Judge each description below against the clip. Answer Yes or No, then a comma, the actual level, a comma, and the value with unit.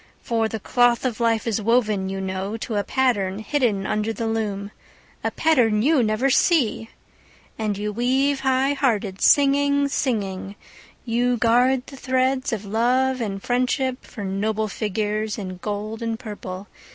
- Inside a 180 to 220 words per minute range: No, average, 150 wpm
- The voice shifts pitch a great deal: No, average, 3.7 semitones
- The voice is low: No, high, 225 Hz